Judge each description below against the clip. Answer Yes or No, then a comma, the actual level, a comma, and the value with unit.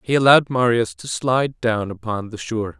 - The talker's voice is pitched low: Yes, low, 115 Hz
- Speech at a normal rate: Yes, average, 195 wpm